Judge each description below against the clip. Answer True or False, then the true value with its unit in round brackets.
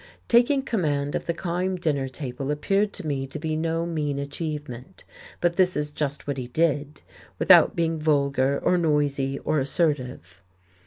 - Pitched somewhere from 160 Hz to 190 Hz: False (150 Hz)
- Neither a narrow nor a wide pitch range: True (3.3 semitones)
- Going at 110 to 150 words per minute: False (160 wpm)